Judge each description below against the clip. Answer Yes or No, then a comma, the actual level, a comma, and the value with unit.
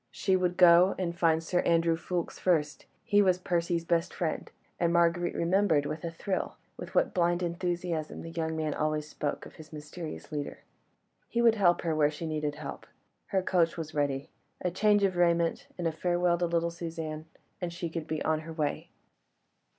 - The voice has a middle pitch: Yes, medium, 170 Hz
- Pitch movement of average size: No, narrow, 2.1 semitones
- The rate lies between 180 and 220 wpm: Yes, average, 190 wpm